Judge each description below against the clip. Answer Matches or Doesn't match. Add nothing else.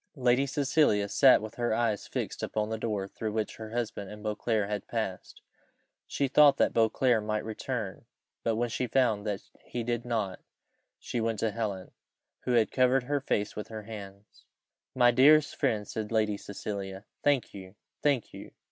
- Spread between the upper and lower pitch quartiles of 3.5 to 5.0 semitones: Doesn't match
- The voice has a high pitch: Doesn't match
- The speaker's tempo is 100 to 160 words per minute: Doesn't match